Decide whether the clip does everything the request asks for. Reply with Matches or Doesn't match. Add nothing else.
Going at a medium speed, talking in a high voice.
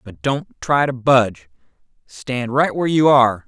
Doesn't match